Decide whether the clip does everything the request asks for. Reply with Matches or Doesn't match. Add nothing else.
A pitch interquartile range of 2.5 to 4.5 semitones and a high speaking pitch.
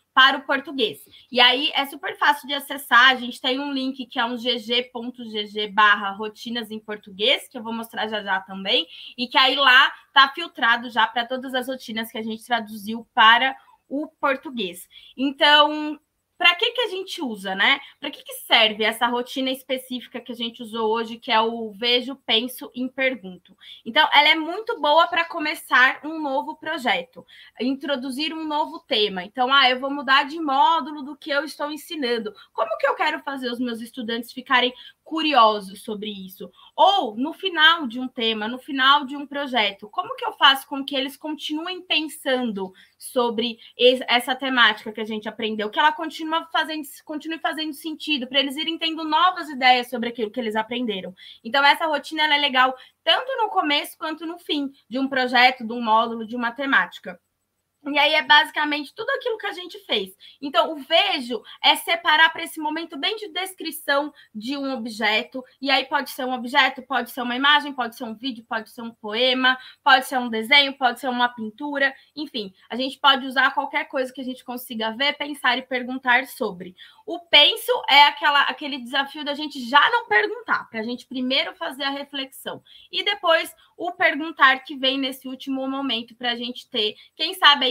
Matches